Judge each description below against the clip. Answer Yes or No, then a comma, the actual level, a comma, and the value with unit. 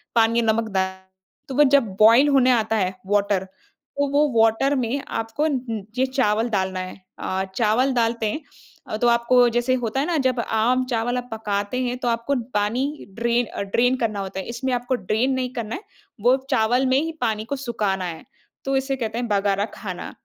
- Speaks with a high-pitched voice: Yes, high, 235 Hz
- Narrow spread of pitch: No, average, 3.2 semitones